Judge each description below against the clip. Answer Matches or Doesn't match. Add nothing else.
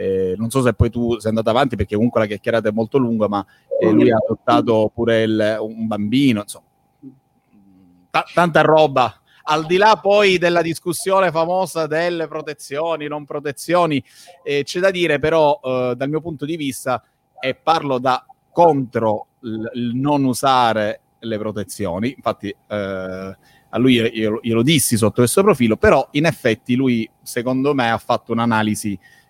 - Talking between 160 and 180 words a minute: Matches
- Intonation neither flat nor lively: Doesn't match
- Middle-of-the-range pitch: Doesn't match